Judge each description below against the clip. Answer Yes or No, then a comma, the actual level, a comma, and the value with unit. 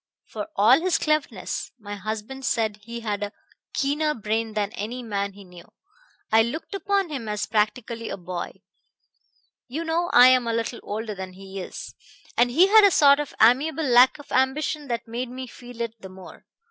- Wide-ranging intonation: No, average, 4.9 semitones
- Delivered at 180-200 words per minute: Yes, average, 185 wpm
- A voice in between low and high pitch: No, high, 235 Hz